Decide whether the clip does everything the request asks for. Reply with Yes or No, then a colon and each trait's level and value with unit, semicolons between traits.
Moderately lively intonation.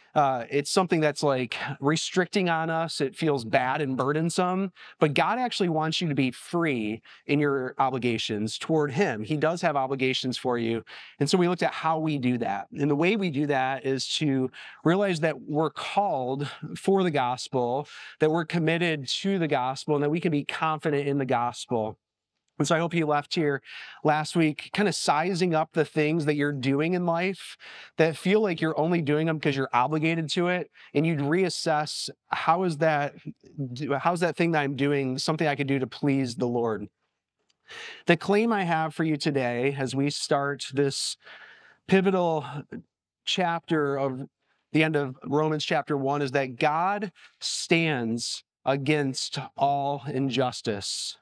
Yes: average, 3.6 semitones